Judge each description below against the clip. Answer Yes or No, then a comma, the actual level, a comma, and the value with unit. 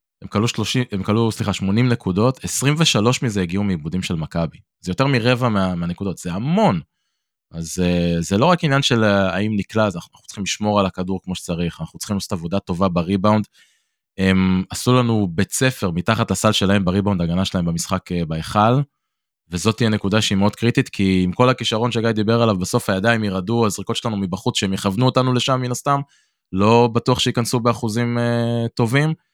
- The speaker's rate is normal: No, fast, 170 wpm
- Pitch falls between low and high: No, low, 105 Hz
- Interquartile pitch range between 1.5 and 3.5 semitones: No, average, 4.1 semitones